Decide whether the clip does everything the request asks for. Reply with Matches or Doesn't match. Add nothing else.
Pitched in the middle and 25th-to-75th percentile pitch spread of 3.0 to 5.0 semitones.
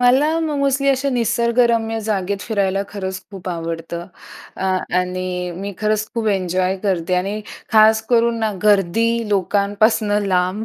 Doesn't match